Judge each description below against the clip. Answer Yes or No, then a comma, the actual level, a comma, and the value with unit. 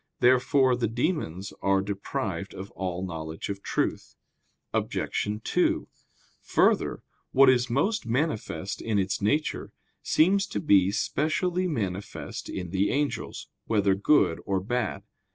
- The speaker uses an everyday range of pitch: No, wide, 6.1 semitones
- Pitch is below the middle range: Yes, low, 105 Hz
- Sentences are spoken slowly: Yes, slow, 125 wpm